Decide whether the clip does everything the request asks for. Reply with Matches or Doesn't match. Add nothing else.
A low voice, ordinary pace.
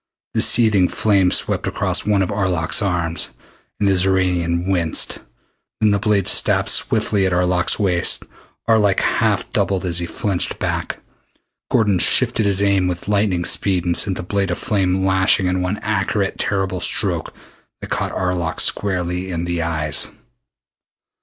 Matches